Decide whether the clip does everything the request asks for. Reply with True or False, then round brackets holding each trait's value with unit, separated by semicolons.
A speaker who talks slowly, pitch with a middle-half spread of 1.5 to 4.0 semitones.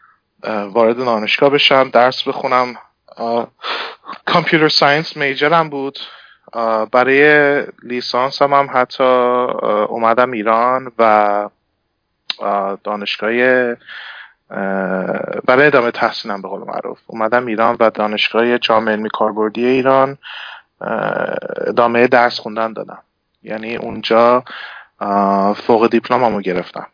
True (95 wpm; 3.3 semitones)